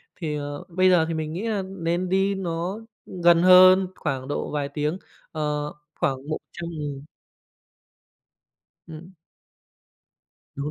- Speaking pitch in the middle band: Yes, medium, 165 Hz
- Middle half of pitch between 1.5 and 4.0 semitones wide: Yes, average, 3.7 semitones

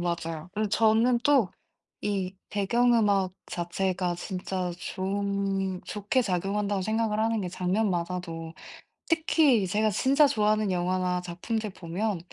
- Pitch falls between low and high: No, high, 195 Hz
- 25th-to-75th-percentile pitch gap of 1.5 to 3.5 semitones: Yes, average, 3.2 semitones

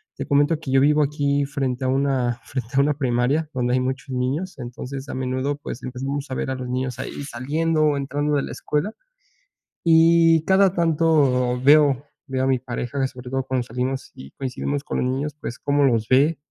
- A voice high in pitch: No, low, 135 Hz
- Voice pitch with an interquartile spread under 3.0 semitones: Yes, narrow, 2.5 semitones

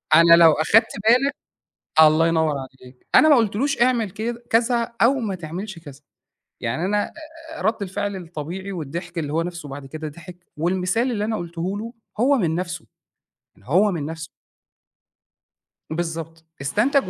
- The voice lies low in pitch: No, medium, 175 Hz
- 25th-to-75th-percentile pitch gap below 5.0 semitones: No, wide, 5.4 semitones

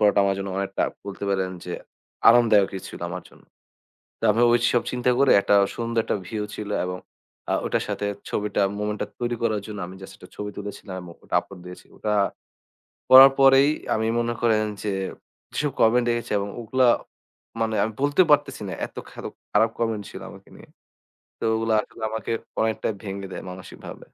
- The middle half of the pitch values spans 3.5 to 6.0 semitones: No, average, 2.9 semitones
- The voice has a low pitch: Yes, low, 110 Hz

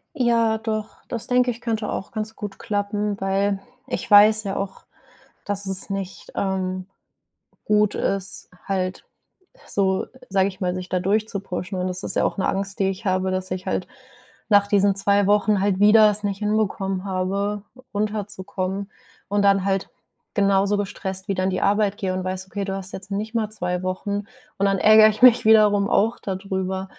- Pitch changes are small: Yes, narrow, 1.7 semitones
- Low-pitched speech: No, high, 200 Hz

